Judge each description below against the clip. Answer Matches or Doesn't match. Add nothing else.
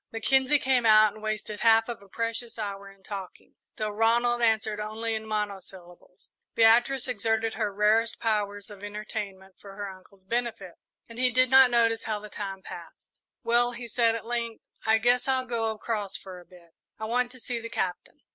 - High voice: Matches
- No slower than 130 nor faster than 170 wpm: Doesn't match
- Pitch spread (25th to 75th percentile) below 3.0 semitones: Matches